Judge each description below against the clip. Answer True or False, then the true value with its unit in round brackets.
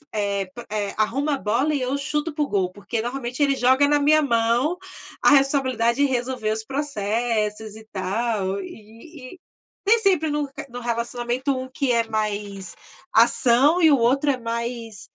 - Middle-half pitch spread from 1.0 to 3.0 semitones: False (4.4 semitones)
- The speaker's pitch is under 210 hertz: False (245 Hz)